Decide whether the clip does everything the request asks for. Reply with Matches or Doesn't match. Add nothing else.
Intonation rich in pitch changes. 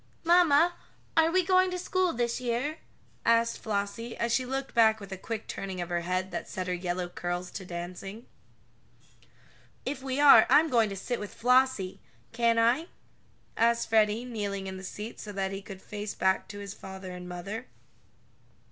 Doesn't match